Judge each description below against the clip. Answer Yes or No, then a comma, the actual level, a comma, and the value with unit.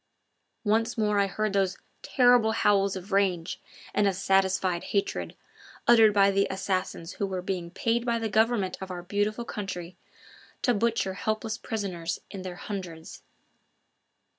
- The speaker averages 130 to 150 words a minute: Yes, average, 145 wpm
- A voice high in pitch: Yes, high, 200 Hz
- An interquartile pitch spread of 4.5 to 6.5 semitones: No, average, 2.7 semitones